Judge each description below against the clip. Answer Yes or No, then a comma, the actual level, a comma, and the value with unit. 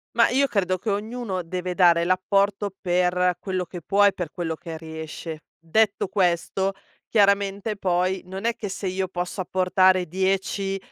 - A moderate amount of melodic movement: No, narrow, 2.0 semitones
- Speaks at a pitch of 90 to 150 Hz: No, medium, 185 Hz